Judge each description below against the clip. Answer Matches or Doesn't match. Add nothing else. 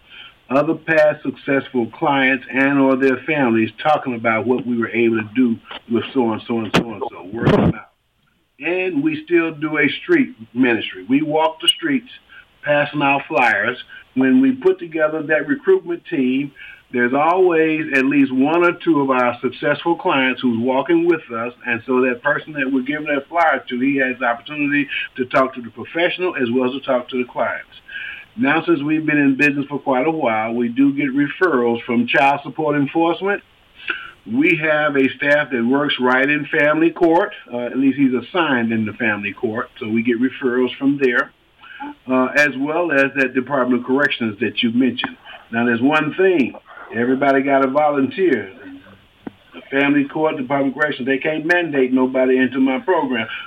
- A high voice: Doesn't match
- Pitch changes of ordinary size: Matches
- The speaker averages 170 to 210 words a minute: Matches